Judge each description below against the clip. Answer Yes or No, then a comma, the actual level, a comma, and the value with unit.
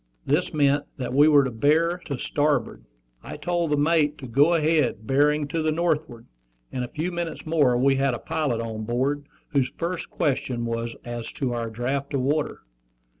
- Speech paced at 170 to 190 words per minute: Yes, average, 185 wpm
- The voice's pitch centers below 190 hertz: Yes, medium, 140 Hz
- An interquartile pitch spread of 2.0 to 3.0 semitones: No, average, 4.0 semitones